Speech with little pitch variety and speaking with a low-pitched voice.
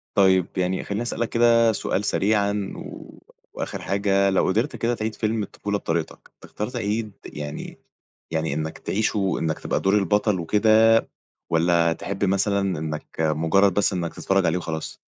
No: average, 3.8 semitones; low, 100 Hz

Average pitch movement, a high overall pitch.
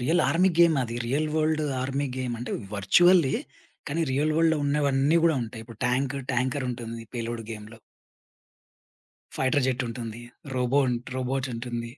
No: average, 4.0 semitones; low, 130 Hz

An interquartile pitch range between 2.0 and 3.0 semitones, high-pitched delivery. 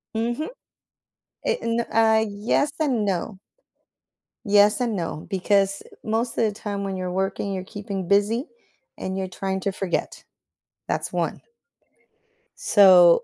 Yes: average, 2.7 semitones; high, 200 Hz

